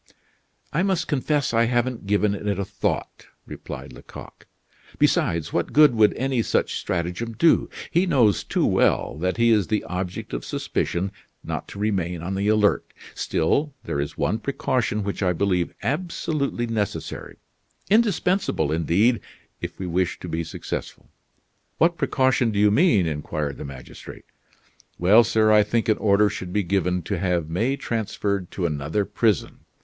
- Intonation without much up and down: No, average, 5.0 semitones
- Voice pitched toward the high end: No, low, 105 Hz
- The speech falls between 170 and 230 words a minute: No, average, 155 wpm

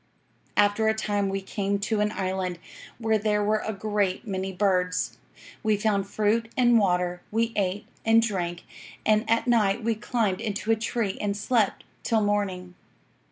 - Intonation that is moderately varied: No, narrow, 2.3 semitones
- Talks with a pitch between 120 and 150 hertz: No, high, 205 Hz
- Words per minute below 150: No, average, 160 wpm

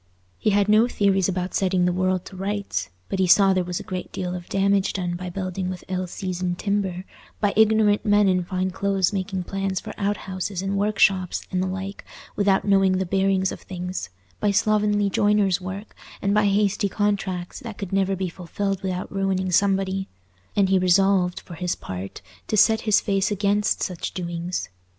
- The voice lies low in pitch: No, high, 190 Hz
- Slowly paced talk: No, average, 180 wpm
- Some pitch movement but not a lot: No, narrow, 1.7 semitones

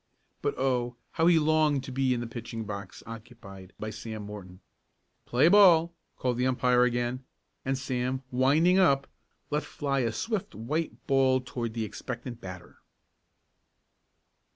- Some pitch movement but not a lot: Yes, average, 3.3 semitones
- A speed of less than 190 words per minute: Yes, average, 145 wpm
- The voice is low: Yes, low, 125 Hz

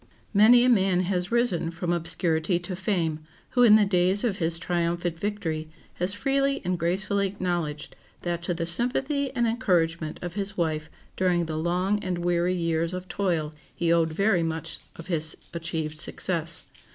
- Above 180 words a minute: No, average, 165 wpm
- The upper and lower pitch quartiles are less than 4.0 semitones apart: Yes, average, 3.1 semitones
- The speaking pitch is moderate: Yes, medium, 175 Hz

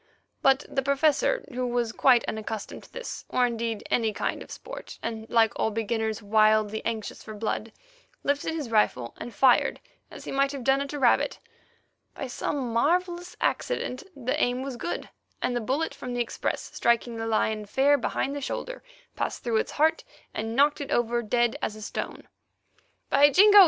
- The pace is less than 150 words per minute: No, average, 180 wpm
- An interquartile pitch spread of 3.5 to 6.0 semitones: Yes, average, 3.9 semitones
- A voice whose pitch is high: Yes, high, 240 Hz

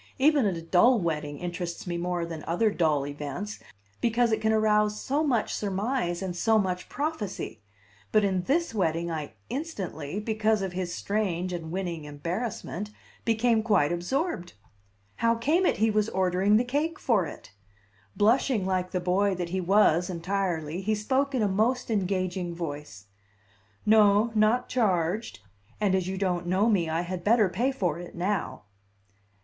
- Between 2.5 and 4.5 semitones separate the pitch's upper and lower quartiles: Yes, average, 4.1 semitones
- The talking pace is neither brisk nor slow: Yes, average, 160 wpm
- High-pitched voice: Yes, high, 195 Hz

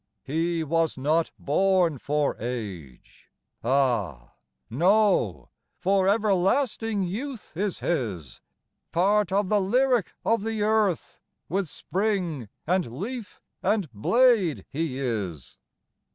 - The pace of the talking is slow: Yes, slow, 105 wpm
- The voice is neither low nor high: Yes, medium, 175 Hz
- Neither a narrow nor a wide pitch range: No, wide, 7.7 semitones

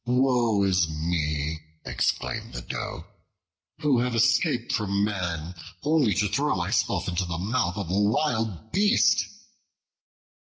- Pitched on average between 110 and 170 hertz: No, low, 100 Hz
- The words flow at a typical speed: No, slow, 125 wpm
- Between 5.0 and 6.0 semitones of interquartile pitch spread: Yes, wide, 5.6 semitones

